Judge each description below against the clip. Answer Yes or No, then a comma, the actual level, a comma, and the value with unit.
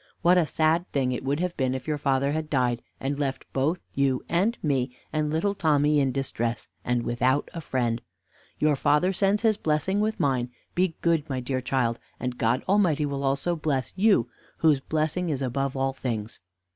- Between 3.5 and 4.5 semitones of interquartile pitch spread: Yes, average, 3.9 semitones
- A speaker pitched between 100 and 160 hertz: Yes, medium, 140 Hz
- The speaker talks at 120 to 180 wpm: No, average, 190 wpm